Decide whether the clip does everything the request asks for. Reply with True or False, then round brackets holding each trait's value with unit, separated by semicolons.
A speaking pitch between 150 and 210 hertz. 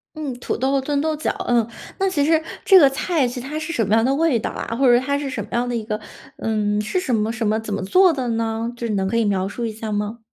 False (240 Hz)